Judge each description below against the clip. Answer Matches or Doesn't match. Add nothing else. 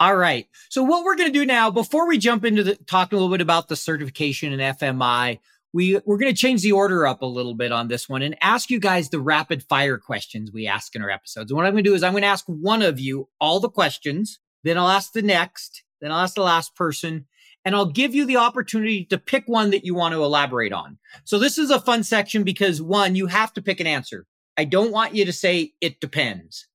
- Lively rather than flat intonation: Matches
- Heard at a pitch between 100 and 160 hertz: Doesn't match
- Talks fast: Matches